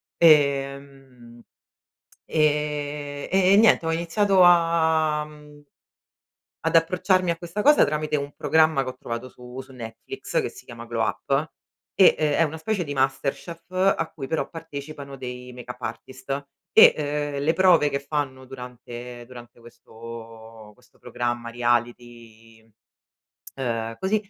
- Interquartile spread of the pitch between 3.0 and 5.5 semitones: Yes, average, 4.8 semitones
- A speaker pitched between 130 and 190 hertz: Yes, medium, 140 Hz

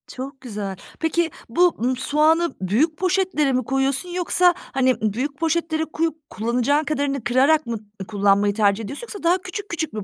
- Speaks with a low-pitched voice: No, very high, 285 Hz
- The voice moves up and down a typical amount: No, wide, 5.8 semitones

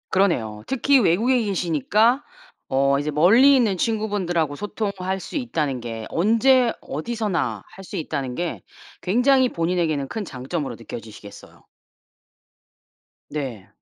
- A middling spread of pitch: No, wide, 7.8 semitones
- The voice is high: No, medium, 180 Hz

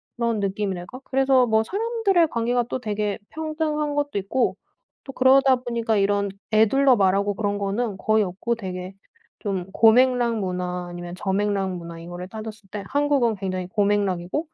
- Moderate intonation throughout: Yes, average, 4.8 semitones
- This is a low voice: No, high, 215 Hz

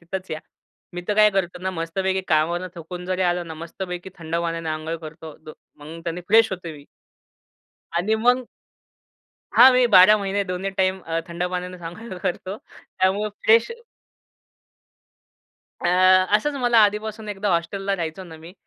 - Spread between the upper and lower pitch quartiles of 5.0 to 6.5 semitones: No, average, 3.1 semitones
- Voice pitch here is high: No, medium, 180 Hz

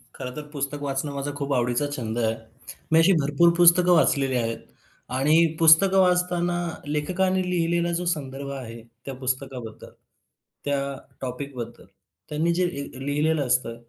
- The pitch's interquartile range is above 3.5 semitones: Yes, average, 4.6 semitones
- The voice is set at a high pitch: No, medium, 145 Hz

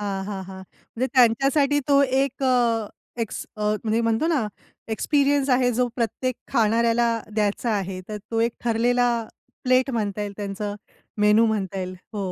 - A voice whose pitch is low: No, high, 230 Hz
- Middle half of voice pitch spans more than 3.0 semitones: Yes, average, 3.4 semitones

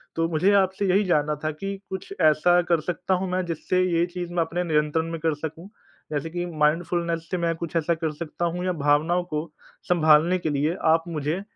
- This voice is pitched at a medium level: Yes, medium, 170 Hz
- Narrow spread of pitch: Yes, narrow, 2.3 semitones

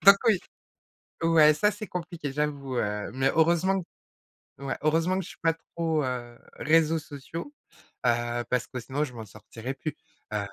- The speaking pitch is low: No, medium, 150 Hz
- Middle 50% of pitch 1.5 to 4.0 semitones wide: No, average, 4.7 semitones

